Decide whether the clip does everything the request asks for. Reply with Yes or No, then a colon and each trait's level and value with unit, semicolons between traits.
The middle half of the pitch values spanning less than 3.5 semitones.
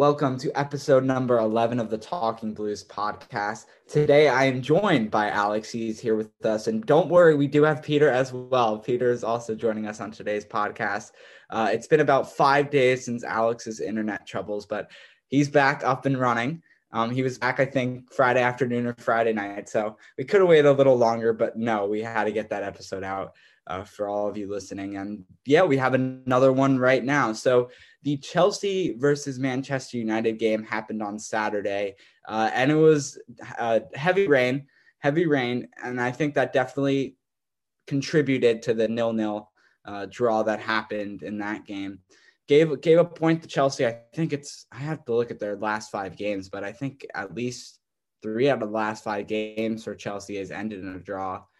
No: average, 4.2 semitones